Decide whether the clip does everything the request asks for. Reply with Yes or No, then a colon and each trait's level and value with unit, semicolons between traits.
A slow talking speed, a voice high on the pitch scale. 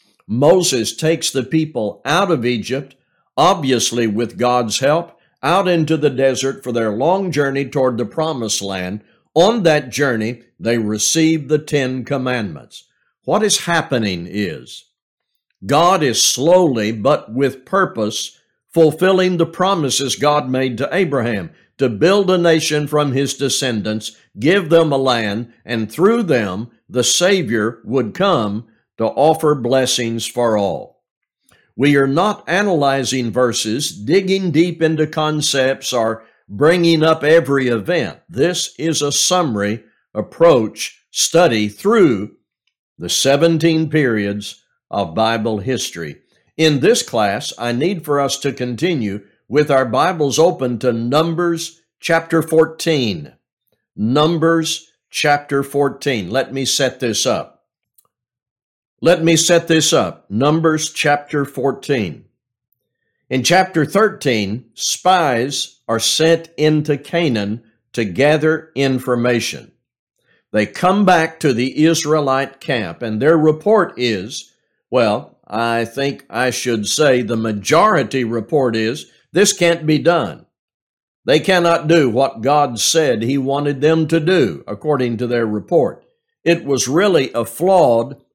No: slow, 125 wpm; medium, 140 Hz